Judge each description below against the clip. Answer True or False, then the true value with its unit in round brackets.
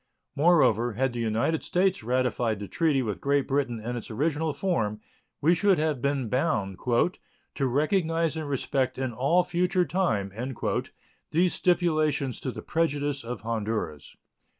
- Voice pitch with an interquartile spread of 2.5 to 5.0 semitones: False (5.6 semitones)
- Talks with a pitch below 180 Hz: True (140 Hz)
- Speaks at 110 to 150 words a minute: True (145 wpm)